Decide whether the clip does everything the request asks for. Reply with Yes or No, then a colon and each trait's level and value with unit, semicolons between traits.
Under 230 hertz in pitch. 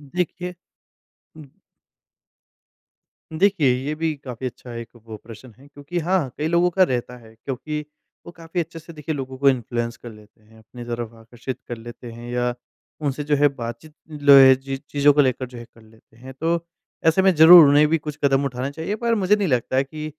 Yes: medium, 140 Hz